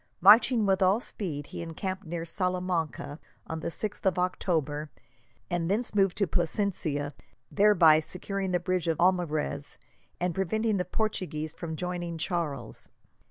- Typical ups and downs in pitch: Yes, average, 3.1 semitones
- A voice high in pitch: No, medium, 180 Hz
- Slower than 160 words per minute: Yes, average, 140 wpm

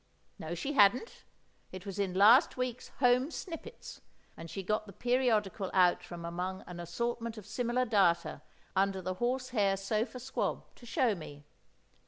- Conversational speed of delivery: Yes, average, 160 wpm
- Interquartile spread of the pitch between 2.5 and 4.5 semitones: No, average, 5.0 semitones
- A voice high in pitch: Yes, high, 210 Hz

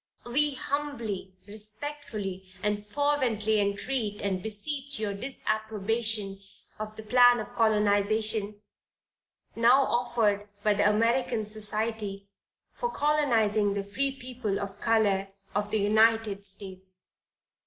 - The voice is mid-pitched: No, high, 215 Hz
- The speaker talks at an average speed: No, slow, 110 wpm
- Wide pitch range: No, average, 2.8 semitones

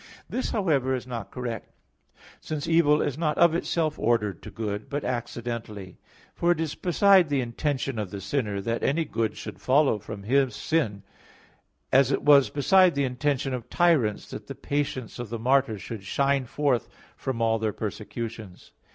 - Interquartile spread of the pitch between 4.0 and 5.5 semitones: Yes, average, 4.8 semitones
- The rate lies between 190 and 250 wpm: No, average, 170 wpm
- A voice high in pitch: No, low, 130 Hz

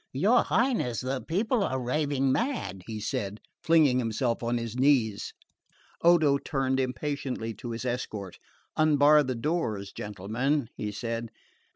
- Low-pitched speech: Yes, low, 130 Hz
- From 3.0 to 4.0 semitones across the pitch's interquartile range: No, average, 4.4 semitones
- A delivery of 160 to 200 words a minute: No, slow, 135 wpm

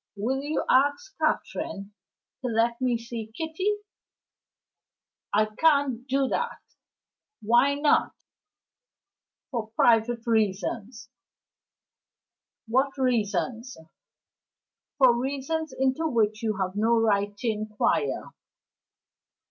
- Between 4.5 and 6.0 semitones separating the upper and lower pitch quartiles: No, average, 4.0 semitones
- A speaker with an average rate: No, slow, 90 wpm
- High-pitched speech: Yes, high, 235 Hz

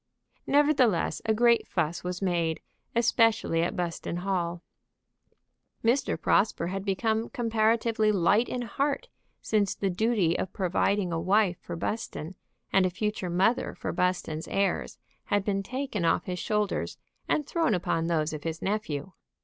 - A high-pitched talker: Yes, high, 195 Hz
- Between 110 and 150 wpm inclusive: Yes, average, 145 wpm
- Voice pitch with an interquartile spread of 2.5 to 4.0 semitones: No, average, 4.4 semitones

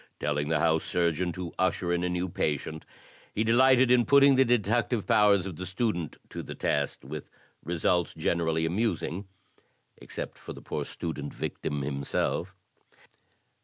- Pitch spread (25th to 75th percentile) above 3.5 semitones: Yes, wide, 5.4 semitones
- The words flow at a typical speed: Yes, average, 150 wpm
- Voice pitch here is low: Yes, very low, 90 Hz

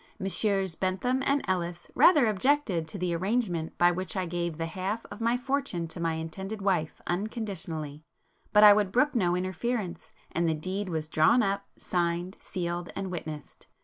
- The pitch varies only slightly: No, average, 3.7 semitones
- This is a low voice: No, medium, 185 Hz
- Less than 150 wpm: No, average, 170 wpm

